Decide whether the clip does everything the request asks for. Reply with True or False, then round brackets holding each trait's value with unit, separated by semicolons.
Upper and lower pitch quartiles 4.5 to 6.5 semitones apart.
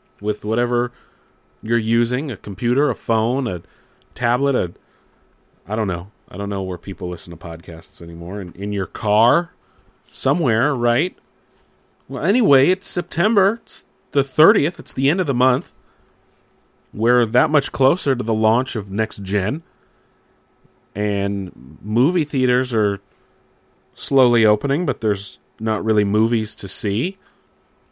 True (5.0 semitones)